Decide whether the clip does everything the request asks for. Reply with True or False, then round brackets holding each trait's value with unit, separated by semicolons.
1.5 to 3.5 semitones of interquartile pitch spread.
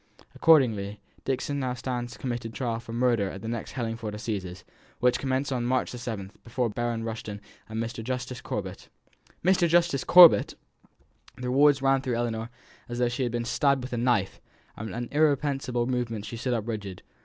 True (2.5 semitones)